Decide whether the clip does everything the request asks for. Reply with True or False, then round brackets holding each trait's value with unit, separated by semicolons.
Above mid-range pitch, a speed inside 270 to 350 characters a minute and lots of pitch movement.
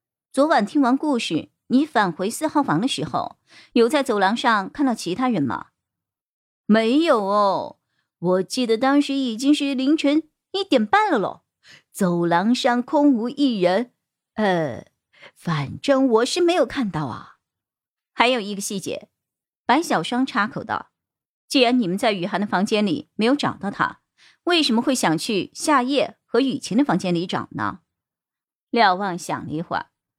False (235 Hz; 225 characters per minute; 6.2 semitones)